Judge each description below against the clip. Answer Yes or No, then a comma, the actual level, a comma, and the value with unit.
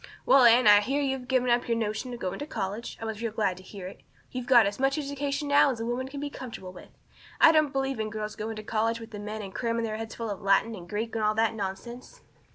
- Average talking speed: No, fast, 275 wpm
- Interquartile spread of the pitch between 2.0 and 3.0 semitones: No, average, 3.5 semitones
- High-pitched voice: Yes, high, 230 Hz